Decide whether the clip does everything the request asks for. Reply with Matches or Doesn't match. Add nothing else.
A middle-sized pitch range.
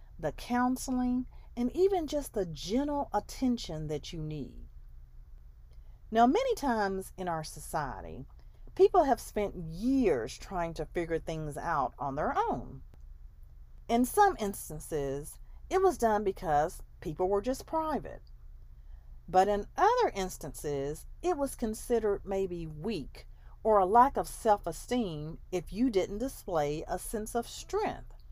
Doesn't match